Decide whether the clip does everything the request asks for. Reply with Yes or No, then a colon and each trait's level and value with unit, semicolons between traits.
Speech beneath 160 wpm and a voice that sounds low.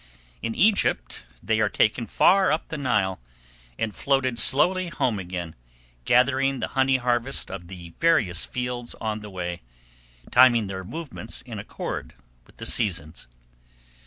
Yes: average, 140 wpm; low, 120 Hz